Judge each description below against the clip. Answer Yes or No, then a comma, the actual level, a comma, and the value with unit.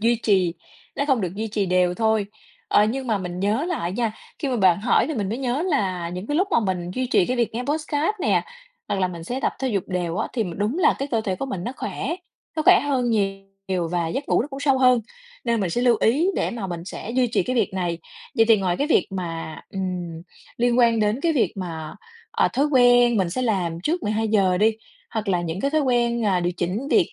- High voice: Yes, high, 220 Hz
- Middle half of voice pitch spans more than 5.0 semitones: Yes, wide, 5.5 semitones